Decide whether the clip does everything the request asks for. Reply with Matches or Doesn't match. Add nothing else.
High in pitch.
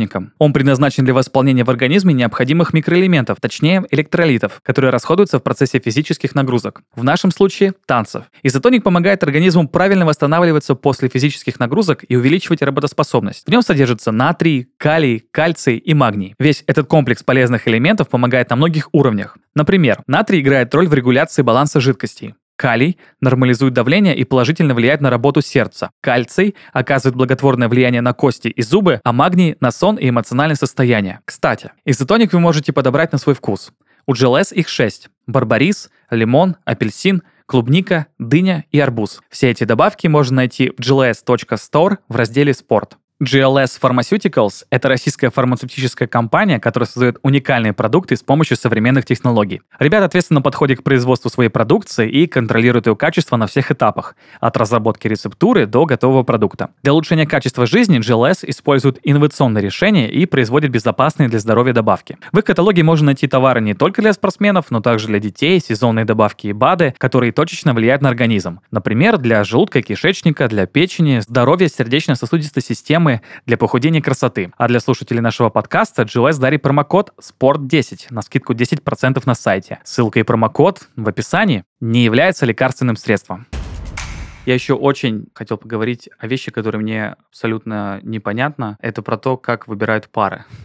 Doesn't match